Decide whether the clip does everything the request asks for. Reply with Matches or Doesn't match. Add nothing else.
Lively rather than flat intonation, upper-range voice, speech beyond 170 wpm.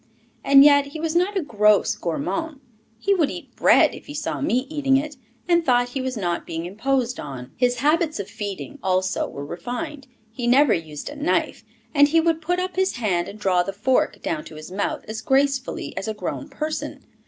Matches